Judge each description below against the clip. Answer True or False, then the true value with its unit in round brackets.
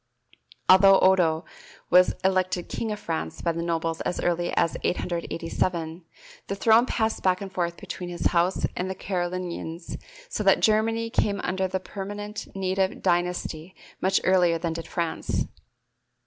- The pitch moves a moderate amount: False (2.1 semitones)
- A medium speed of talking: True (150 wpm)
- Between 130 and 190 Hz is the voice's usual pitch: True (185 Hz)